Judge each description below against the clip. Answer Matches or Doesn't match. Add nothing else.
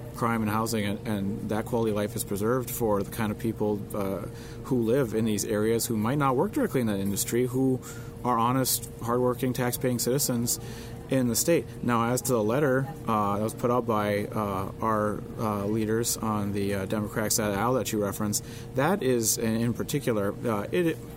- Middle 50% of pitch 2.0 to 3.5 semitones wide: Matches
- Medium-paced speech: Matches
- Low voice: Matches